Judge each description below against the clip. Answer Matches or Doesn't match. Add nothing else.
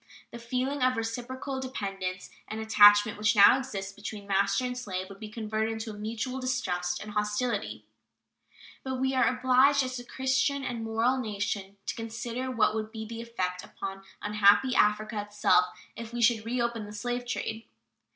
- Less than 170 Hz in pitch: Doesn't match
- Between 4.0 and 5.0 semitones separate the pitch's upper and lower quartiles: Doesn't match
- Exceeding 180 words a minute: Doesn't match